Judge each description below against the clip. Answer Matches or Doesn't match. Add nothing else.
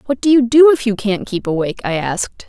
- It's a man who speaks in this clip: Doesn't match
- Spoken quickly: Matches